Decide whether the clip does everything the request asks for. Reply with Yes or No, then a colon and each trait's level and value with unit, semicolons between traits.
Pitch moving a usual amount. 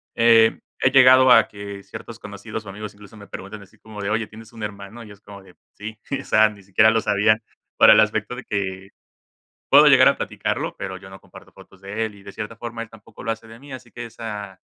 No: narrow, 2.1 semitones